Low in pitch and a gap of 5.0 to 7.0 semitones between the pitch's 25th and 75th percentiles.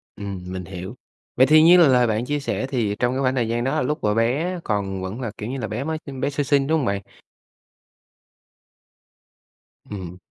Yes: low, 125 Hz; wide, 5.4 semitones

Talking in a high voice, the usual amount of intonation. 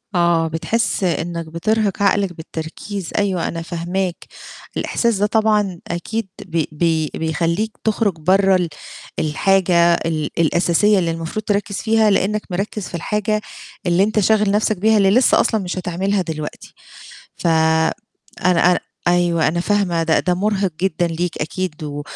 No: medium, 180 Hz; average, 3.7 semitones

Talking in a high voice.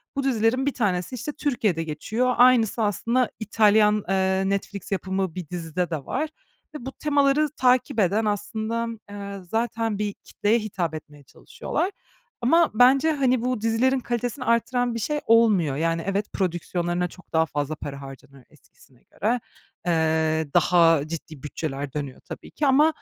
Yes: high, 210 Hz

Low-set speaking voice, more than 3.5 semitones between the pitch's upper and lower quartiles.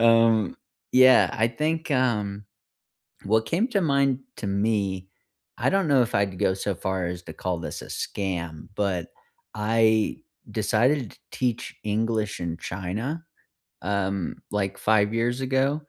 Yes: low, 110 Hz; average, 4.8 semitones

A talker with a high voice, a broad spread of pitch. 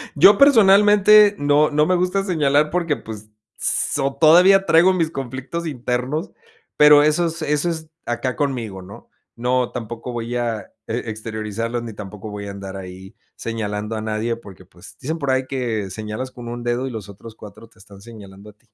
No: low, 125 Hz; wide, 6.1 semitones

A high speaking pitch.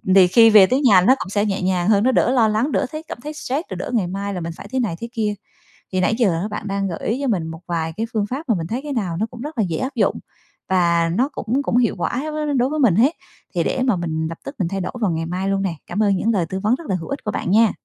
Yes: high, 205 Hz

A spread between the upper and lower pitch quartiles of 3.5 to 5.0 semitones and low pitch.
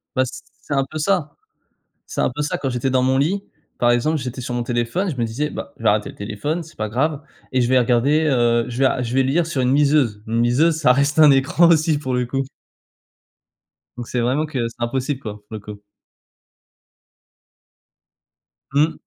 Yes: average, 3.9 semitones; low, 130 Hz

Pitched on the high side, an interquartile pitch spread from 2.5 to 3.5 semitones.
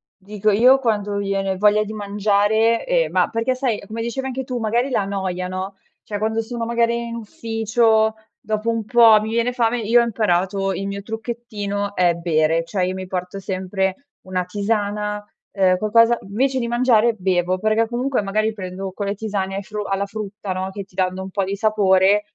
Yes: high, 210 Hz; average, 2.9 semitones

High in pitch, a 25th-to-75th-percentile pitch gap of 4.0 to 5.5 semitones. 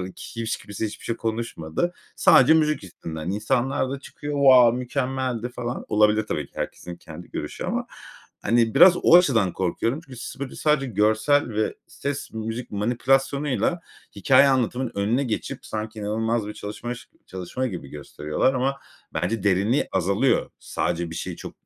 No: low, 115 Hz; average, 4.4 semitones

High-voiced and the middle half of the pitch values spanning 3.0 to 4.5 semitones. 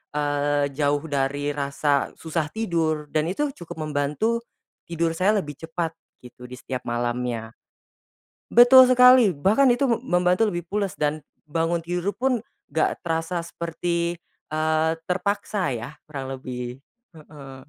No: medium, 160 Hz; average, 4.0 semitones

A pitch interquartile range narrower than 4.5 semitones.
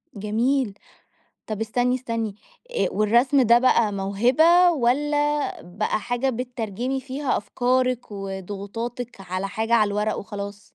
Yes: average, 3.9 semitones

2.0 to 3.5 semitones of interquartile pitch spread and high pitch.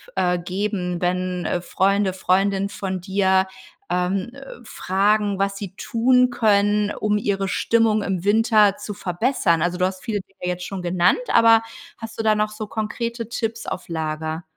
Yes: average, 2.8 semitones; high, 200 Hz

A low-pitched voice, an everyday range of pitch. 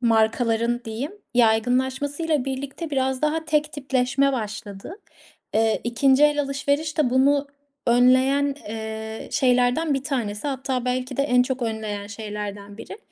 No: very high, 255 Hz; average, 3.9 semitones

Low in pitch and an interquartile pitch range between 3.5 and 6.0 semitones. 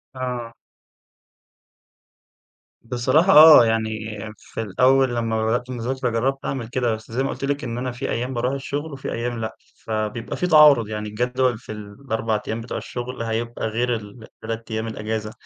No: low, 120 Hz; narrow, 2.5 semitones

